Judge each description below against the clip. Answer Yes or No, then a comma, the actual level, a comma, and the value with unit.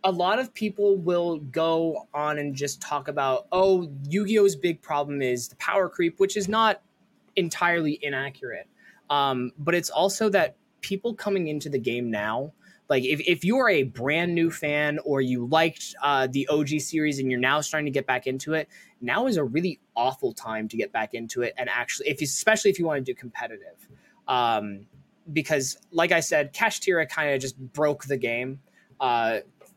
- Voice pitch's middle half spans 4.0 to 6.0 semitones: Yes, average, 5.0 semitones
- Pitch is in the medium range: Yes, medium, 150 Hz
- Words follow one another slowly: No, average, 190 wpm